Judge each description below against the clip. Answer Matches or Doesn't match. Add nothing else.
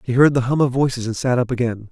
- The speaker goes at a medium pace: Doesn't match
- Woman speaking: Doesn't match